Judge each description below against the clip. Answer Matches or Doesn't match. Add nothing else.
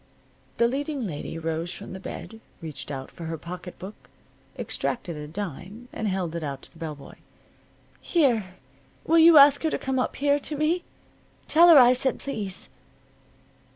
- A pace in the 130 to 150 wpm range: Doesn't match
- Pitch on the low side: Doesn't match